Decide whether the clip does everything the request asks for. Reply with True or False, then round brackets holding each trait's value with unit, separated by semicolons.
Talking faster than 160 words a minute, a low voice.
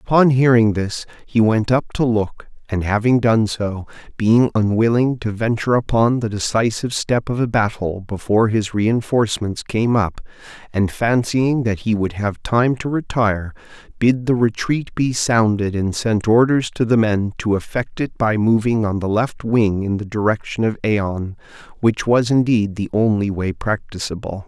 True (170 wpm; 110 Hz)